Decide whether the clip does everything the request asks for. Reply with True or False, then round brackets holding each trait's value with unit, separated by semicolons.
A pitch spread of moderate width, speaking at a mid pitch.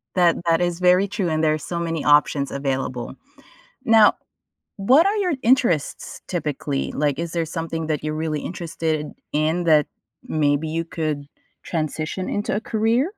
True (3.2 semitones; 165 Hz)